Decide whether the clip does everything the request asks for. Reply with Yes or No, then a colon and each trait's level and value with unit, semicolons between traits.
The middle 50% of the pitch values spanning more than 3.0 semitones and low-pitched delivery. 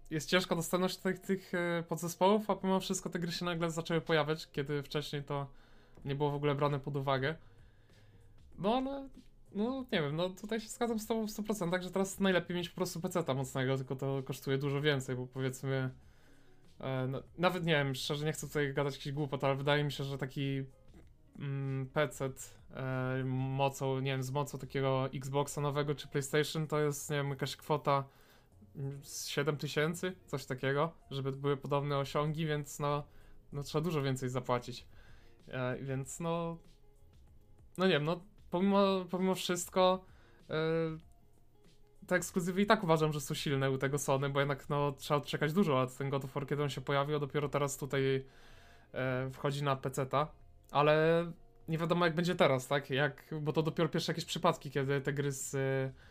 No: average, 3.7 semitones; medium, 145 Hz